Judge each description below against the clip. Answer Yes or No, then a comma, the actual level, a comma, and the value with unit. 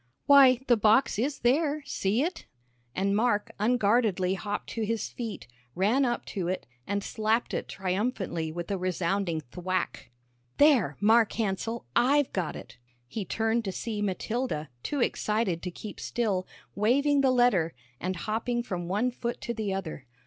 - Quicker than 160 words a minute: No, average, 155 wpm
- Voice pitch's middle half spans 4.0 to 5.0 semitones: Yes, average, 4.5 semitones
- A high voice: Yes, high, 215 Hz